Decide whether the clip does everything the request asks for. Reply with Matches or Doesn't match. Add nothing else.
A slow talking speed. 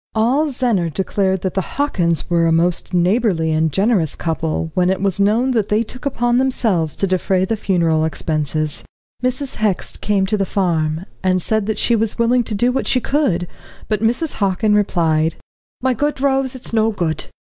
Doesn't match